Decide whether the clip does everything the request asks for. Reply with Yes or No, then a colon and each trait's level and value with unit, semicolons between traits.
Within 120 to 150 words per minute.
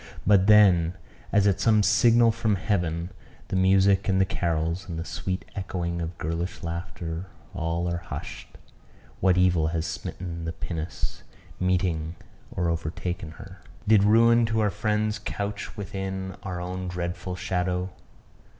Yes: average, 140 wpm